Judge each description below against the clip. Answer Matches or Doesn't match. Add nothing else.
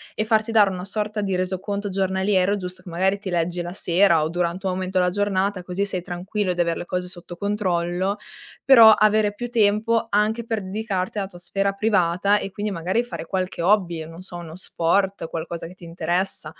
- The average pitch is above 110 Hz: Matches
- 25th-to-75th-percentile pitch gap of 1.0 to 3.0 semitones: Matches